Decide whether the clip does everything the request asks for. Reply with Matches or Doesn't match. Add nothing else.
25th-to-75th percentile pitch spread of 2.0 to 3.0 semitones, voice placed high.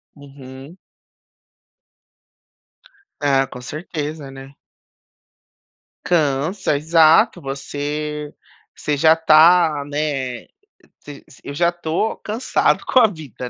Doesn't match